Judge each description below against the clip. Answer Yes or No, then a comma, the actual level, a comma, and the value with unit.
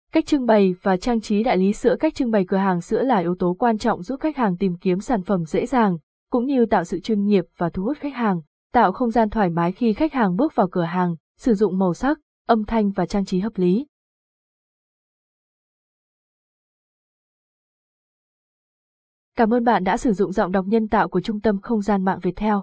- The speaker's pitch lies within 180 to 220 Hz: Yes, high, 215 Hz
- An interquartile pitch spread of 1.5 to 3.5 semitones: No, average, 4.1 semitones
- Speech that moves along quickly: No, average, 210 wpm